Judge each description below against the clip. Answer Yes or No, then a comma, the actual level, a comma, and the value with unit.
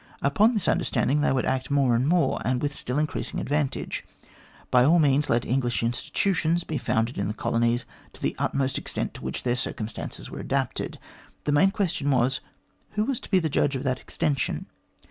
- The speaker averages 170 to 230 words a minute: Yes, average, 190 wpm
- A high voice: No, low, 135 Hz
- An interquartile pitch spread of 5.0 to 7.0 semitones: No, average, 4.1 semitones